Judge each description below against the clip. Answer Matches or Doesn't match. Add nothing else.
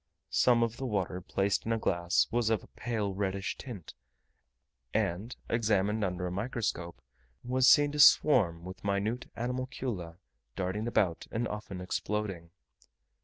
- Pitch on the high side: Doesn't match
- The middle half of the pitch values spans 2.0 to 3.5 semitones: Doesn't match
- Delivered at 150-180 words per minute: Doesn't match